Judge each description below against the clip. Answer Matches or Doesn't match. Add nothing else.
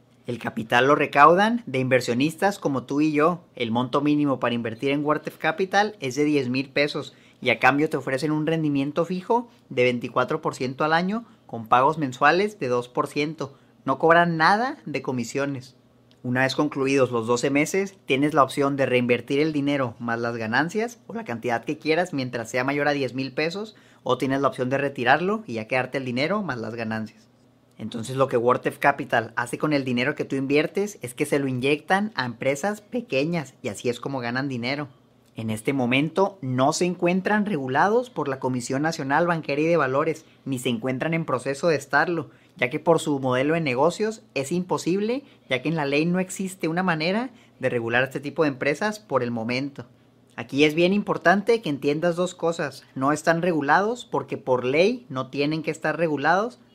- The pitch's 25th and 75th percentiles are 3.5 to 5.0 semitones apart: Matches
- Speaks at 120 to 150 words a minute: Doesn't match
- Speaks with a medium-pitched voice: Matches